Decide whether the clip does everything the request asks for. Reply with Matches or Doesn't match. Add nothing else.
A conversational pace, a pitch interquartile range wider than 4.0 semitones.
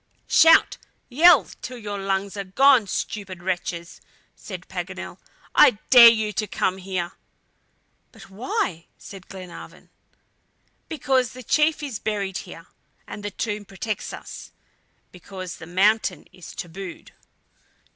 Doesn't match